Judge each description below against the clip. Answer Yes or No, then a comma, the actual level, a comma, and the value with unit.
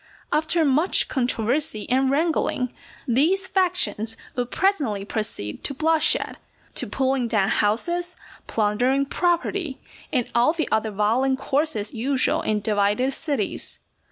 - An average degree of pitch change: No, wide, 6.2 semitones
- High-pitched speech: Yes, very high, 265 Hz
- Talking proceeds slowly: Yes, slow, 120 wpm